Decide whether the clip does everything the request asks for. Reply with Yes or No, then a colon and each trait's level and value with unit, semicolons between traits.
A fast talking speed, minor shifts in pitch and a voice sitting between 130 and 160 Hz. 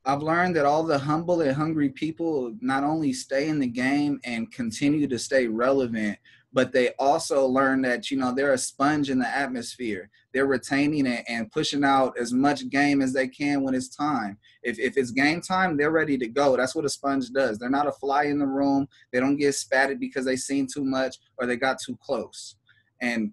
Yes: fast, 215 wpm; narrow, 2.1 semitones; low, 135 Hz